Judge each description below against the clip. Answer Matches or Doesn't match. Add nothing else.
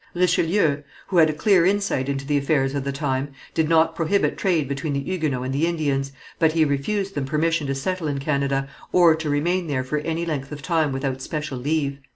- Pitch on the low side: Doesn't match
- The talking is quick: Matches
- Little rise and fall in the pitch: Doesn't match